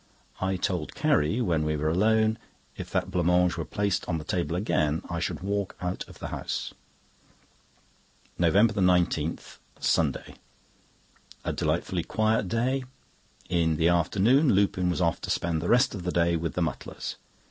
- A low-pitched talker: Yes, very low, 90 Hz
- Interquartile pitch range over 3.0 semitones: Yes, average, 3.4 semitones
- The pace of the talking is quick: No, average, 160 wpm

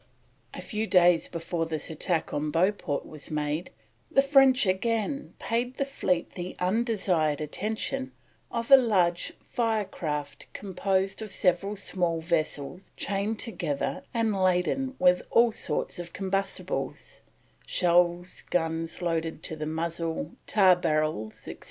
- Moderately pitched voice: Yes, medium, 180 Hz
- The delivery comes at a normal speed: No, slow, 130 wpm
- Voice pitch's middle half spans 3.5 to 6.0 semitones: Yes, average, 4.7 semitones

